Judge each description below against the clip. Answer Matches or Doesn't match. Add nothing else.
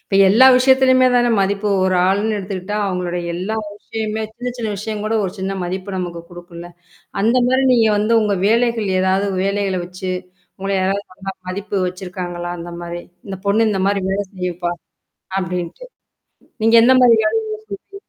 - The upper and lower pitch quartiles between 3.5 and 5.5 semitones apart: Doesn't match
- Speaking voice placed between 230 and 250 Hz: Doesn't match